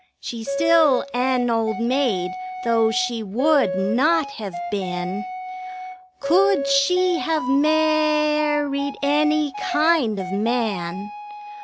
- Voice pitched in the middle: No, very high, 270 Hz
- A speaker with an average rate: No, slow, 115 wpm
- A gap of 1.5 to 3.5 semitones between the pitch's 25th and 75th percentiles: No, wide, 5.5 semitones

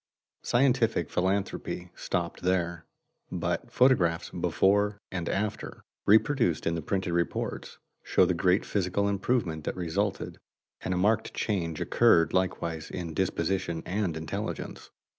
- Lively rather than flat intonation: No, average, 3.3 semitones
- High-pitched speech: No, very low, 95 Hz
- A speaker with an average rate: No, slow, 120 wpm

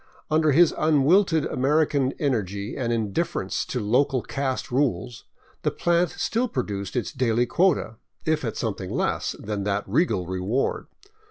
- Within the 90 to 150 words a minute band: Yes, average, 140 wpm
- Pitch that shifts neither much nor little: No, wide, 6.5 semitones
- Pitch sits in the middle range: No, low, 130 Hz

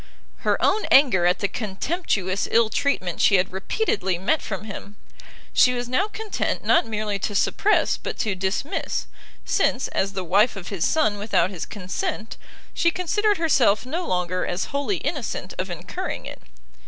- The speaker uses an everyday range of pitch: No, wide, 7.4 semitones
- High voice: Yes, high, 210 Hz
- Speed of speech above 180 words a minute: No, average, 165 wpm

